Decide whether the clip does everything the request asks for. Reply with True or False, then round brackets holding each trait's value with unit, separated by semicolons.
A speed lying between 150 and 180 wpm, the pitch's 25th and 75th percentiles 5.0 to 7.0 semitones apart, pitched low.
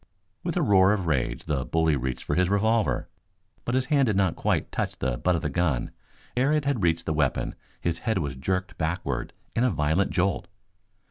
False (205 wpm; 5.4 semitones; 90 Hz)